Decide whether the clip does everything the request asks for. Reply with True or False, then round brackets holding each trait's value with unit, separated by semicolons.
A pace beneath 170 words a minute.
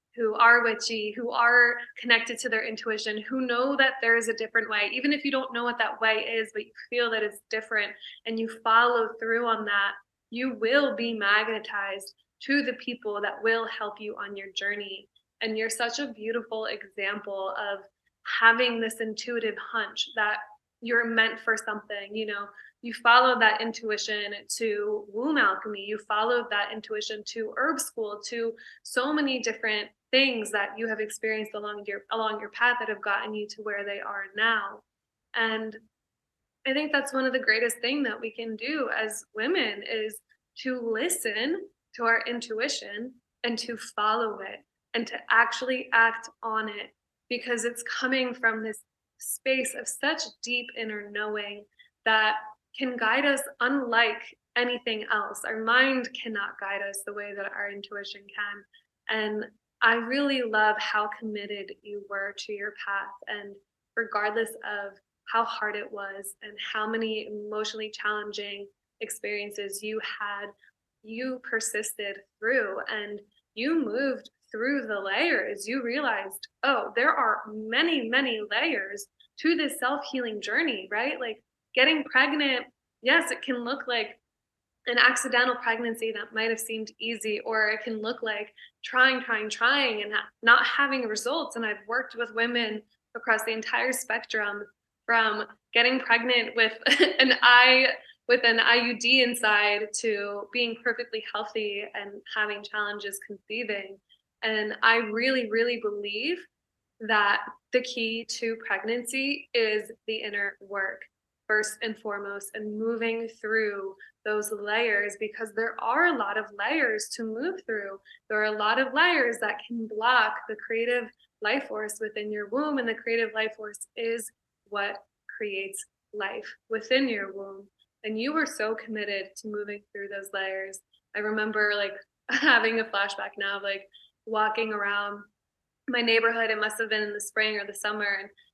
True (160 wpm)